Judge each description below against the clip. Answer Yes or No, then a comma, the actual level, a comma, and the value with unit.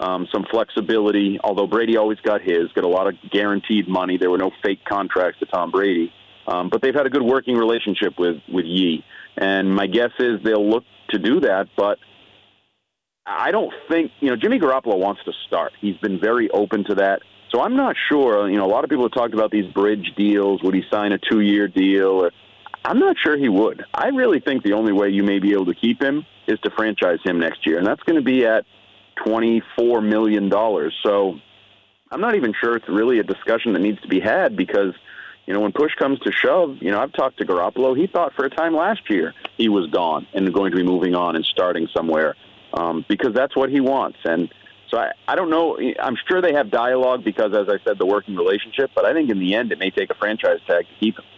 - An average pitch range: Yes, average, 3.5 semitones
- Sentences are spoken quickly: Yes, fast, 235 wpm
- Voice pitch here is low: Yes, low, 105 Hz